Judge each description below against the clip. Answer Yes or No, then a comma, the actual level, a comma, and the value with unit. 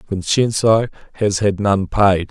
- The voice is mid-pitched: No, low, 100 Hz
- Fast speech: No, slow, 130 wpm